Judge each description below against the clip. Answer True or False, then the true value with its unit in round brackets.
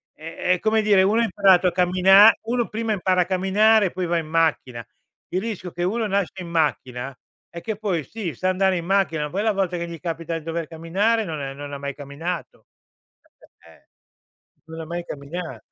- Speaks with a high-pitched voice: False (180 Hz)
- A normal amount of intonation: True (3.4 semitones)